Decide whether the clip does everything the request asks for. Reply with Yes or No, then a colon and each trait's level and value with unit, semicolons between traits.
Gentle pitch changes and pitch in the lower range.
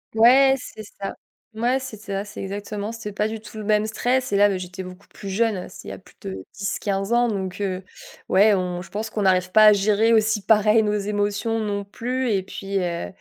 No: narrow, 2.1 semitones; high, 205 Hz